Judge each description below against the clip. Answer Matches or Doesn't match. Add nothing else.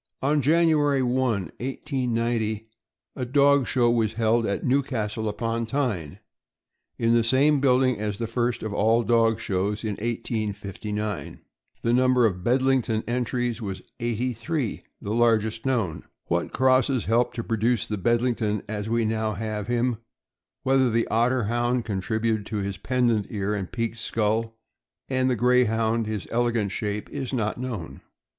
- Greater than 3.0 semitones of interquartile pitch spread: Doesn't match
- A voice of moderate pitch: Doesn't match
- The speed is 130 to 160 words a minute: Matches